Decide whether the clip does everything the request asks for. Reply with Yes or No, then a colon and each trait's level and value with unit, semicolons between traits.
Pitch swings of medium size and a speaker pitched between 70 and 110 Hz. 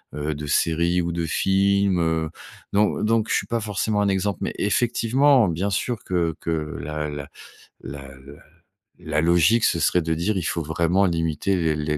Yes: average, 4.2 semitones; very low, 85 Hz